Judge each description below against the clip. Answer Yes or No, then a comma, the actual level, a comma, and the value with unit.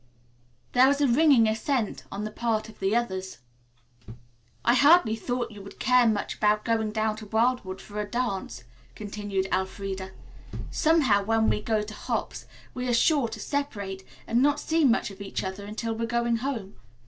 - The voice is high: Yes, high, 220 Hz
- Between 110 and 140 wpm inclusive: No, average, 175 wpm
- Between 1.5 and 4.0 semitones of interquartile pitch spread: Yes, average, 3.4 semitones